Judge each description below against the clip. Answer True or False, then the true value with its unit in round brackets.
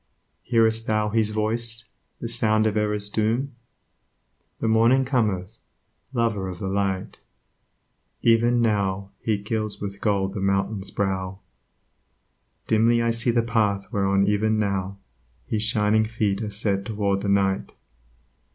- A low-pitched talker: True (105 Hz)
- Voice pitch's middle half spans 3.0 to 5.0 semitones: False (2.4 semitones)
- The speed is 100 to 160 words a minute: True (135 wpm)